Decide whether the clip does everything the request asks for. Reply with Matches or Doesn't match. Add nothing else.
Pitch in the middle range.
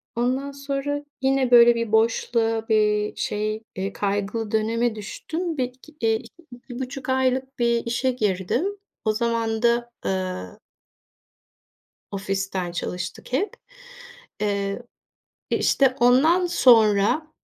Doesn't match